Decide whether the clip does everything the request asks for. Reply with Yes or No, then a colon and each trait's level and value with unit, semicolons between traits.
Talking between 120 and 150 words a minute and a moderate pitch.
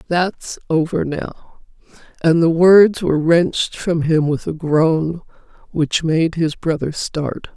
Yes: average, 145 wpm; medium, 160 Hz